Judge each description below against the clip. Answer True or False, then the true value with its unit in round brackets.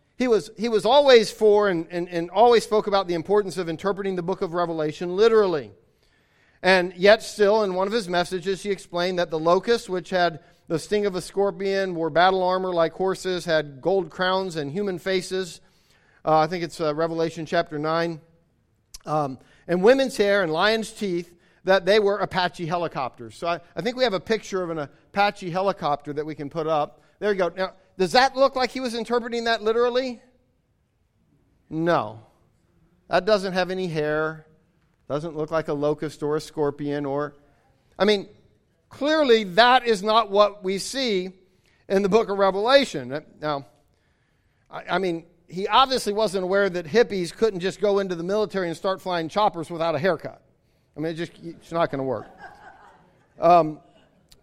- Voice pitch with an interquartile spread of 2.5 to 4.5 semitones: True (4.0 semitones)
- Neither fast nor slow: True (180 wpm)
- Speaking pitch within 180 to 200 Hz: True (185 Hz)